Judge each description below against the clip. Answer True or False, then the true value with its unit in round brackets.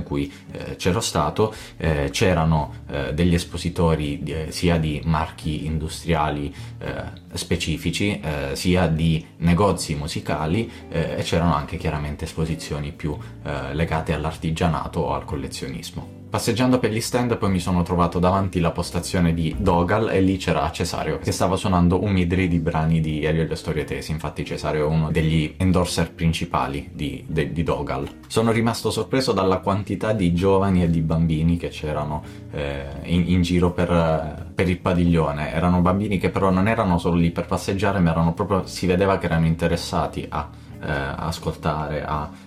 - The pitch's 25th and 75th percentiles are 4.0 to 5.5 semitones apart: False (2.9 semitones)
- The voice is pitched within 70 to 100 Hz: True (85 Hz)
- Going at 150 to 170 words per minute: True (155 wpm)